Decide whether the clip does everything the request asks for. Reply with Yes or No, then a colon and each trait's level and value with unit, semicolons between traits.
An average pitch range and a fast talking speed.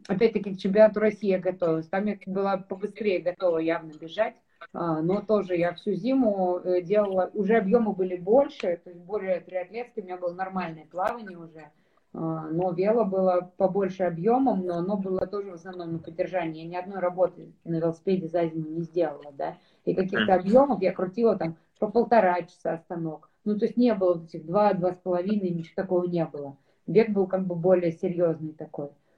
Yes: average, 3.2 semitones; fast, 180 wpm